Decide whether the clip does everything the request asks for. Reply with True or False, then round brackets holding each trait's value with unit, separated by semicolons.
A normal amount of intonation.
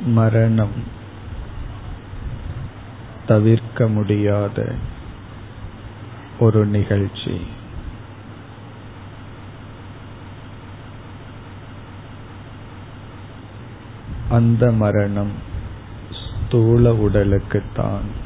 False (1.9 semitones)